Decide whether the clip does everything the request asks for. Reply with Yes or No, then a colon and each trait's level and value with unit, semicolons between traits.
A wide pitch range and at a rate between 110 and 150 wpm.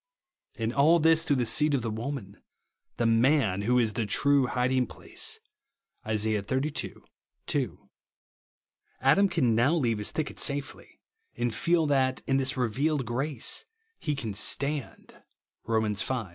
No: average, 4.5 semitones; average, 145 wpm